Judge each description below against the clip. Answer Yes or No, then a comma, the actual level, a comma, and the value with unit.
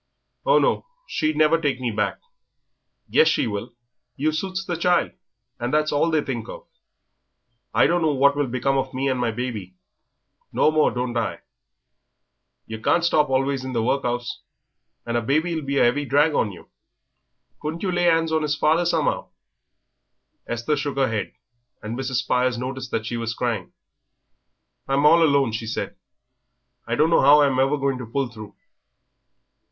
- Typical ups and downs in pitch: Yes, average, 4.2 semitones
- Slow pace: No, average, 170 wpm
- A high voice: No, low, 135 Hz